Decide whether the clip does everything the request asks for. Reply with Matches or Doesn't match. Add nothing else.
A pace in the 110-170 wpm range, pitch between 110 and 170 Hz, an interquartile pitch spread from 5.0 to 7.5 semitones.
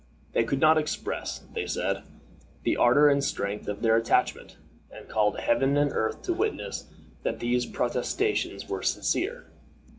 Matches